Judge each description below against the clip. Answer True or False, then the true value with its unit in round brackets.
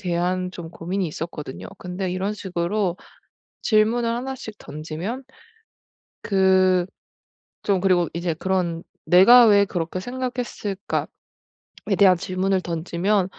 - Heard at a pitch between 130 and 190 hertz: True (185 Hz)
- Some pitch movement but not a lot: True (3.0 semitones)